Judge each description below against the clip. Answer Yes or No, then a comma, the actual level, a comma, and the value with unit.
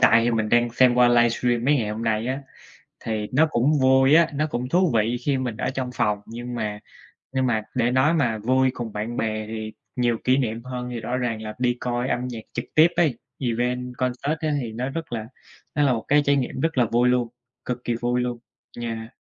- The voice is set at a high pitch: No, low, 125 Hz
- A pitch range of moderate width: No, narrow, 2.1 semitones